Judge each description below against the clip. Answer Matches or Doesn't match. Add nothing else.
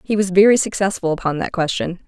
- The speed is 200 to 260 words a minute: Matches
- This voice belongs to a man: Doesn't match